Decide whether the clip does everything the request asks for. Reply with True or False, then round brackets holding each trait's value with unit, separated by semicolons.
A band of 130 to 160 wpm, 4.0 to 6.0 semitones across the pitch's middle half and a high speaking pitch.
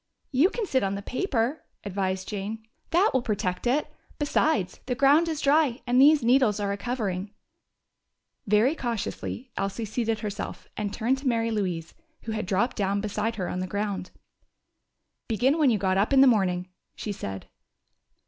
False (170 wpm; 4.8 semitones; 220 Hz)